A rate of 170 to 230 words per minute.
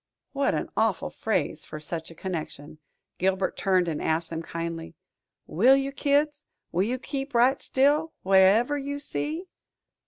No: average, 150 wpm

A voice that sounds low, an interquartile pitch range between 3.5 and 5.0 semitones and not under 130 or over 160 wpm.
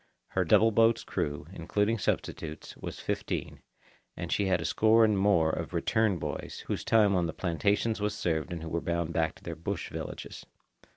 No: very low, 90 Hz; average, 4.3 semitones; average, 185 wpm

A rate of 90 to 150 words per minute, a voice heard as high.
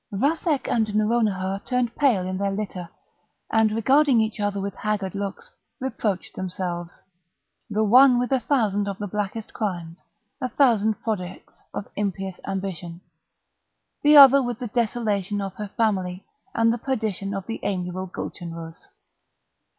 Yes: slow, 135 wpm; high, 205 Hz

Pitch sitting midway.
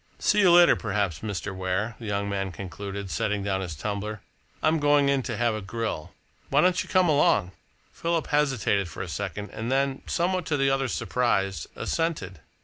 No: low, 110 Hz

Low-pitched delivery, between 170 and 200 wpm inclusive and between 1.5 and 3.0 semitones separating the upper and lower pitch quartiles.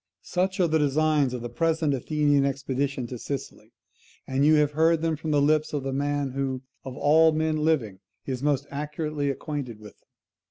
No: medium, 145 Hz; average, 190 wpm; narrow, 2.4 semitones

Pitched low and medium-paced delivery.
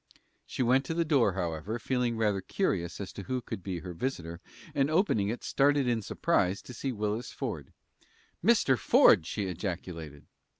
Yes: low, 110 Hz; average, 175 wpm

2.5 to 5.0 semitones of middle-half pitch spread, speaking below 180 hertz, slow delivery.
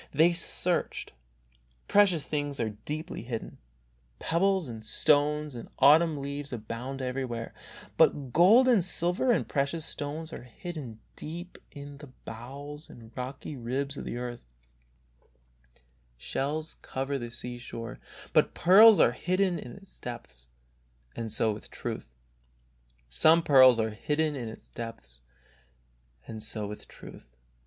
No: wide, 5.4 semitones; medium, 140 Hz; slow, 110 wpm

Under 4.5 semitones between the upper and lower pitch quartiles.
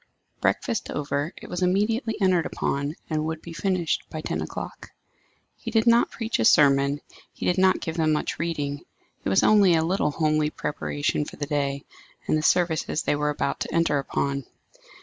Yes: average, 4.1 semitones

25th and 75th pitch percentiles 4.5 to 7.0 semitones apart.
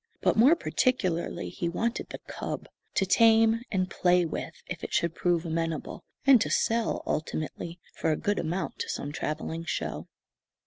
Yes: wide, 5.4 semitones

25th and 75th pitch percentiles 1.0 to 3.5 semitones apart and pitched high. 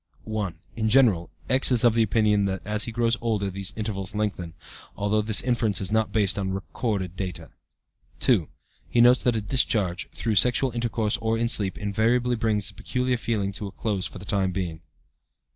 No: average, 3.0 semitones; low, 105 Hz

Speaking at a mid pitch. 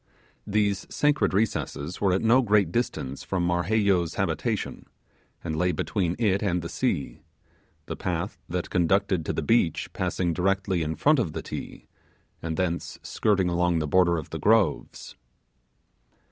No: very low, 90 Hz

